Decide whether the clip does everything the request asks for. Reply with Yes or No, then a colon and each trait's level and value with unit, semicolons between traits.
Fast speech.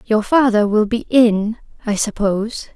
No: average, 155 wpm